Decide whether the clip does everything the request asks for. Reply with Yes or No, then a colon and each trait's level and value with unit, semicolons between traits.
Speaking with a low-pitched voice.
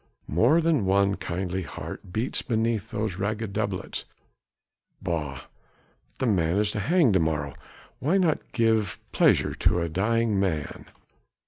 Yes: low, 100 Hz